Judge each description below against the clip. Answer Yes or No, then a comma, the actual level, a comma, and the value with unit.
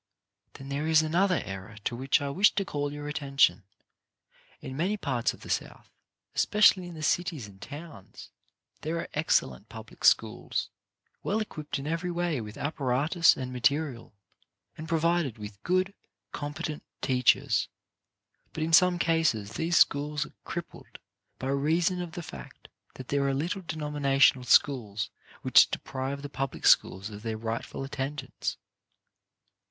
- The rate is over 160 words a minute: No, average, 150 wpm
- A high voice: No, medium, 145 Hz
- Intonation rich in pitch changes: No, average, 4.3 semitones